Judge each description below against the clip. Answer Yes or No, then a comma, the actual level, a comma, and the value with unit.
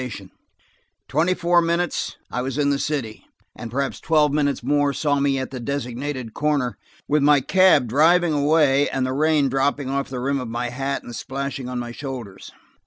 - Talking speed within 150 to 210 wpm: Yes, average, 185 wpm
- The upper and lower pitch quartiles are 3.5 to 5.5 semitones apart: No, average, 2.7 semitones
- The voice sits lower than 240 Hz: Yes, medium, 140 Hz